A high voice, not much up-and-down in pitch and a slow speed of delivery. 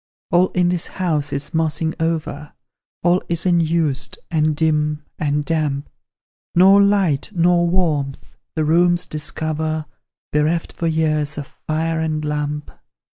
No: medium, 160 Hz; narrow, 2.3 semitones; slow, 125 wpm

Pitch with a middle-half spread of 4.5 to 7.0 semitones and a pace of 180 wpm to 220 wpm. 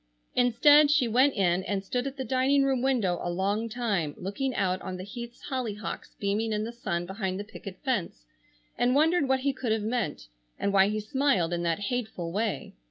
Yes: average, 5.1 semitones; average, 200 wpm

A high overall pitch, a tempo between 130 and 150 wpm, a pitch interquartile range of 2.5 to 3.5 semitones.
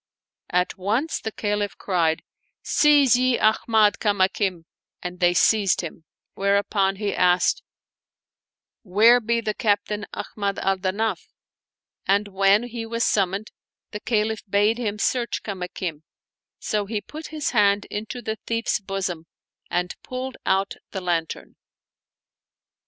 Yes: high, 205 Hz; slow, 135 wpm; average, 2.9 semitones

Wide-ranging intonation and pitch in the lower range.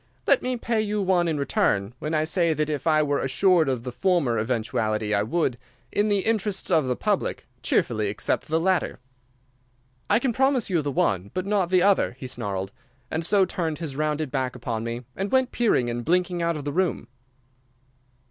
No: wide, 7.1 semitones; medium, 155 Hz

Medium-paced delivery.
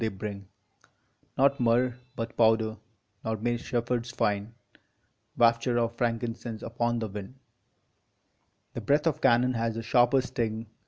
No: slow, 130 wpm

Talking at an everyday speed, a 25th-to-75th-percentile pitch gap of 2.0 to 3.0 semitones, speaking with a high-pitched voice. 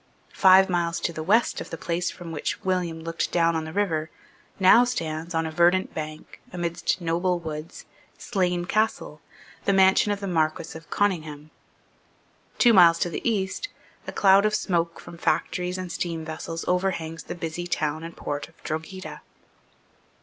No: average, 165 wpm; narrow, 2.6 semitones; medium, 170 Hz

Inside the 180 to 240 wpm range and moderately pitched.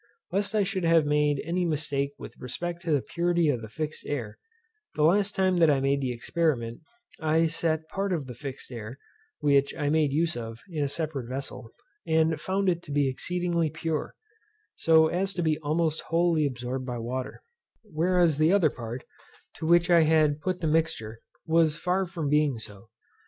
Yes: average, 185 wpm; medium, 155 Hz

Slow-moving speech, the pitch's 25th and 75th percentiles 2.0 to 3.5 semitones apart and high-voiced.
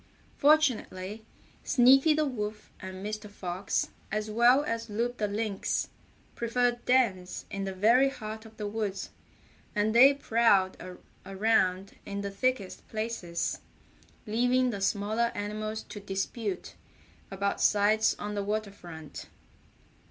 Yes: slow, 125 wpm; average, 3.0 semitones; high, 215 Hz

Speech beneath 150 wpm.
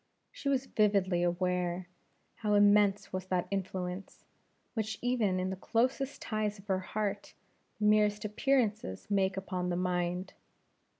Yes: slow, 135 wpm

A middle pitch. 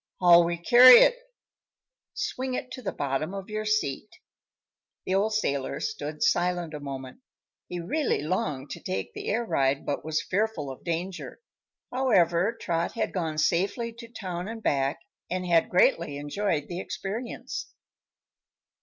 Yes: medium, 175 Hz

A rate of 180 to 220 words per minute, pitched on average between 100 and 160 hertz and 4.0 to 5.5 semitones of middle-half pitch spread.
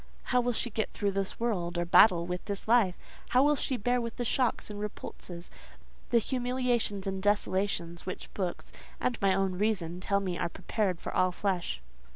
No: average, 185 wpm; high, 200 Hz; average, 4.4 semitones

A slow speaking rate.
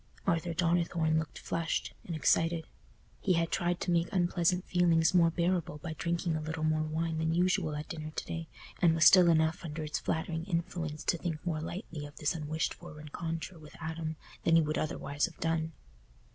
No: average, 190 wpm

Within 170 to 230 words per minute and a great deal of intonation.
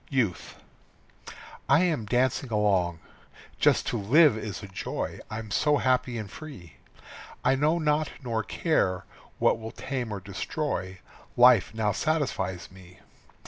No: slow, 135 wpm; wide, 6.2 semitones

